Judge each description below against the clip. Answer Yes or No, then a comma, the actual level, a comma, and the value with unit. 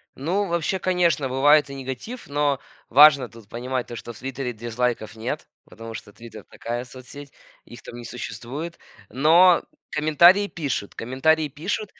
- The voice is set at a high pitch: No, low, 135 Hz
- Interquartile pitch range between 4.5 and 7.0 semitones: Yes, average, 4.8 semitones